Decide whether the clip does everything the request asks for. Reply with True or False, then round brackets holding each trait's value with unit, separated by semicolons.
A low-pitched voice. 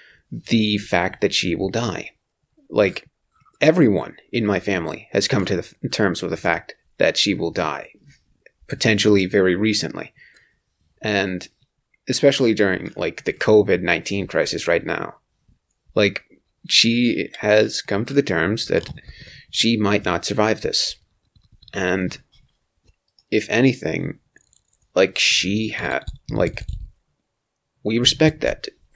True (100 Hz)